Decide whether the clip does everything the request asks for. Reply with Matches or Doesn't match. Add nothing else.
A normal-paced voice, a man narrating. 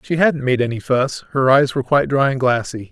Doesn't match